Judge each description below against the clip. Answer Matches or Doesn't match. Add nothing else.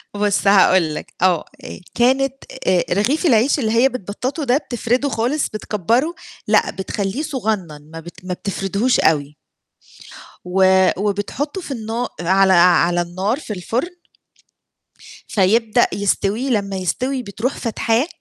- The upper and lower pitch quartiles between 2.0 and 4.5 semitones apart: Doesn't match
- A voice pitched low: Doesn't match